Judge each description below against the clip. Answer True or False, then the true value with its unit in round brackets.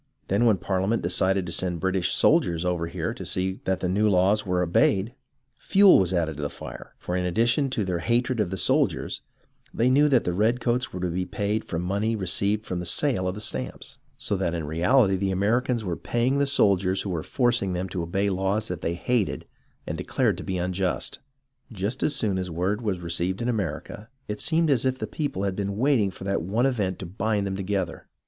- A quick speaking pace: True (220 wpm)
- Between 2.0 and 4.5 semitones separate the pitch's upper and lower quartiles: True (3.9 semitones)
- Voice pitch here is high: False (95 Hz)